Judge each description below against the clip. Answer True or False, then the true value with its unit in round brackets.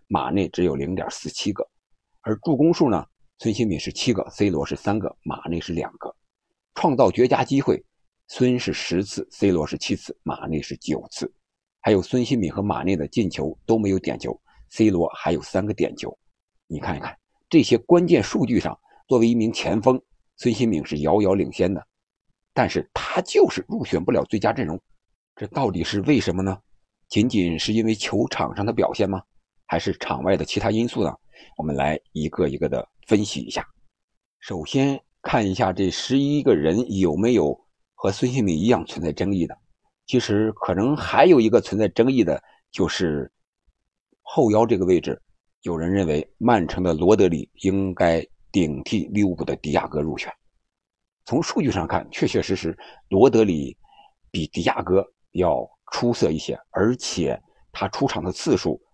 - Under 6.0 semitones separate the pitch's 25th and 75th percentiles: True (5.6 semitones)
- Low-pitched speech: True (105 Hz)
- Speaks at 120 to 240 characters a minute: False (255 characters per minute)